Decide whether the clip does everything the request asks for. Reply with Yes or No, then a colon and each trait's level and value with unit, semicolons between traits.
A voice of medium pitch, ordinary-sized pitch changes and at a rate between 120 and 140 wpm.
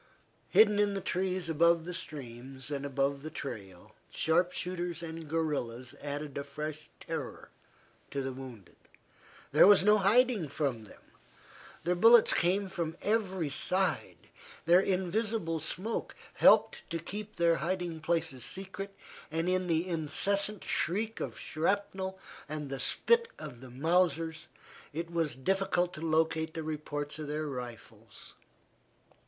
Yes: medium, 165 Hz; average, 4.4 semitones; slow, 135 wpm